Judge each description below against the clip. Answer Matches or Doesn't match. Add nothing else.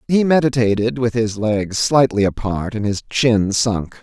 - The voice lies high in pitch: Doesn't match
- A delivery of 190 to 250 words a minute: Doesn't match